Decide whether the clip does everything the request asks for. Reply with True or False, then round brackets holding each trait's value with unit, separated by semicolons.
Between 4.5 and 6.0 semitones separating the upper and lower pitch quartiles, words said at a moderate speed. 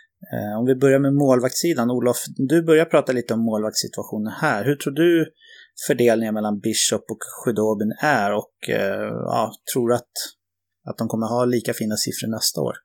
True (4.8 semitones; 170 wpm)